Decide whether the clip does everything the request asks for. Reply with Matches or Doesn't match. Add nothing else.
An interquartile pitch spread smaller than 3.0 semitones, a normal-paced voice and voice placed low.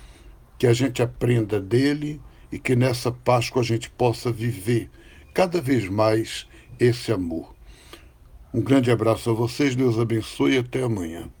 Matches